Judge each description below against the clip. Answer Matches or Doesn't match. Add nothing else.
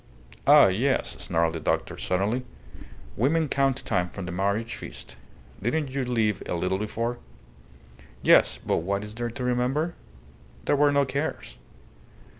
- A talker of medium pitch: Doesn't match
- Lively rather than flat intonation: Matches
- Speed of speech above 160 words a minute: Doesn't match